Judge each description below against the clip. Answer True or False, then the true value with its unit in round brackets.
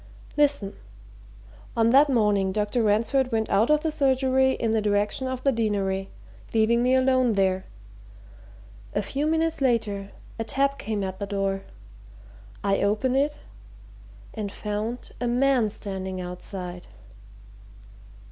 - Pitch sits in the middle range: False (220 Hz)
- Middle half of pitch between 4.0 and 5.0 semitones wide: True (4.7 semitones)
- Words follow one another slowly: True (130 wpm)